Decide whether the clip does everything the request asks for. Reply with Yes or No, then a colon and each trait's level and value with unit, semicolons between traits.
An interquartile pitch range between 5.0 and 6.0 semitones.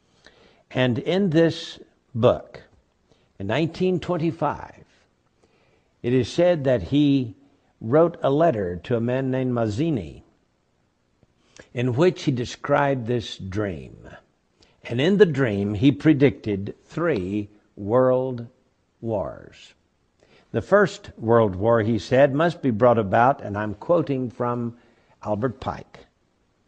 Yes: average, 5.3 semitones